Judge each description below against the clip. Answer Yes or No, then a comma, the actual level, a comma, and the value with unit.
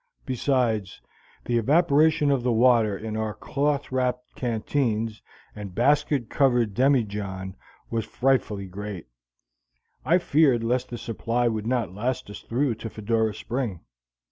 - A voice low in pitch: Yes, low, 120 Hz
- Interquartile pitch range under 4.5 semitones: Yes, average, 3.4 semitones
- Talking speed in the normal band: No, slow, 130 wpm